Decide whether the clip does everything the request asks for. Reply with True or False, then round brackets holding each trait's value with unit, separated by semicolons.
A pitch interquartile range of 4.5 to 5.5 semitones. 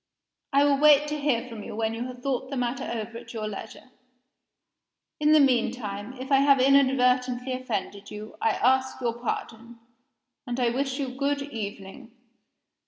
False (3.0 semitones)